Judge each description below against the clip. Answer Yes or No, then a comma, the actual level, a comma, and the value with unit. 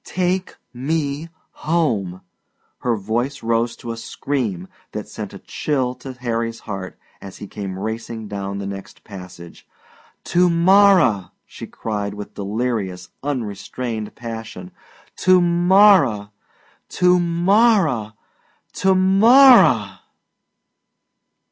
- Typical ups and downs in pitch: No, wide, 8.9 semitones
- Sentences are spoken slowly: Yes, slow, 105 wpm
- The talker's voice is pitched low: Yes, low, 120 Hz